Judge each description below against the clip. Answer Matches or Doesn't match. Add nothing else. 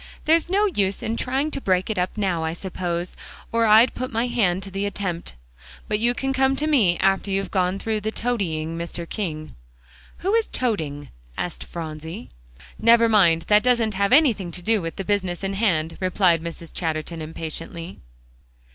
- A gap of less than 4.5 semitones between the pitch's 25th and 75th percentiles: Doesn't match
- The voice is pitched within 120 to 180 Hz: Doesn't match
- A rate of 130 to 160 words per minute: Doesn't match